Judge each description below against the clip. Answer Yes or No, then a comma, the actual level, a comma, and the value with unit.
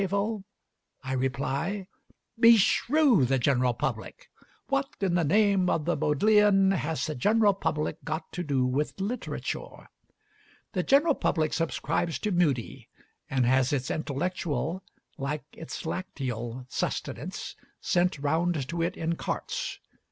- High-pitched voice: No, medium, 165 Hz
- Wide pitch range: Yes, wide, 6.1 semitones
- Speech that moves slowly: Yes, slow, 125 wpm